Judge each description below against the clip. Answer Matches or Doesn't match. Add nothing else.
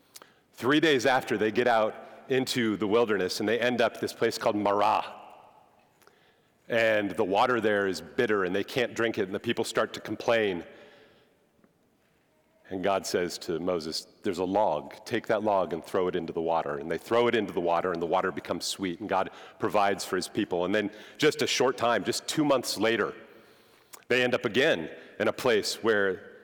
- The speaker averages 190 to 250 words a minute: Matches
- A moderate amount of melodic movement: Matches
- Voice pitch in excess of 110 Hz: Doesn't match